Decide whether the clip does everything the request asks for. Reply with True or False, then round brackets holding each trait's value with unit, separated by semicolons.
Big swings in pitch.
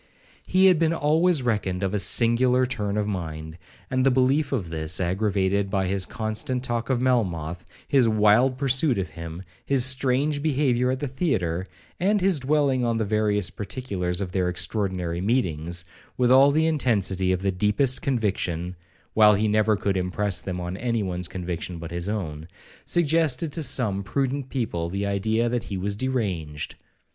True (5.9 semitones)